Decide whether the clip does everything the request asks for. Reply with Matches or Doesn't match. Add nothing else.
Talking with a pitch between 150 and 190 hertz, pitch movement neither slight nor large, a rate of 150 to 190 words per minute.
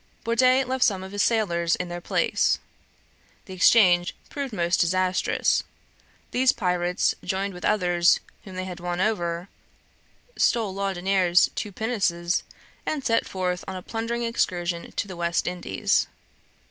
Doesn't match